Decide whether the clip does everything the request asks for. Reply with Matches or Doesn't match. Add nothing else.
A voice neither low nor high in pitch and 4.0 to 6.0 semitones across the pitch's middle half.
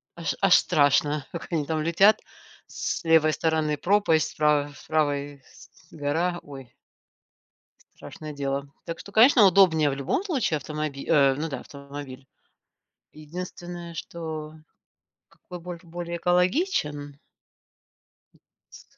Doesn't match